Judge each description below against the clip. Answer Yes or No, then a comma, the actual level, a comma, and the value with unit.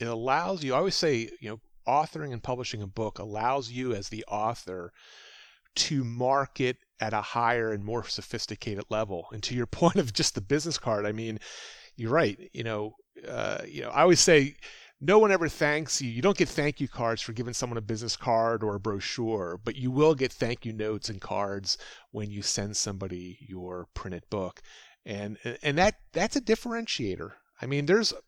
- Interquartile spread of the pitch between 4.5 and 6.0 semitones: Yes, average, 4.8 semitones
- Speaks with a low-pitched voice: Yes, low, 115 Hz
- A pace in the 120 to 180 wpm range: No, average, 195 wpm